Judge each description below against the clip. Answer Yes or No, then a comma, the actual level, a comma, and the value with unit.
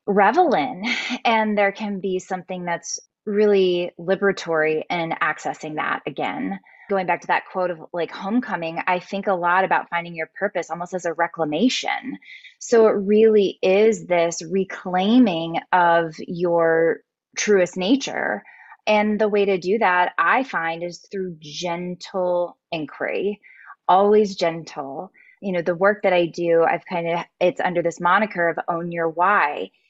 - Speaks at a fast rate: No, average, 155 wpm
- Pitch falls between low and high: Yes, medium, 180 Hz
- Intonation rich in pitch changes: No, average, 3.2 semitones